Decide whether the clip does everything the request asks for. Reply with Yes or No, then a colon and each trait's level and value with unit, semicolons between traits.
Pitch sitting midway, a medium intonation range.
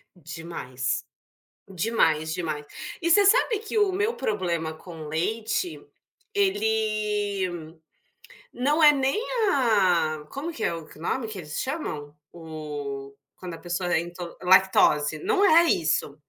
No: medium, 180 Hz; wide, 8.7 semitones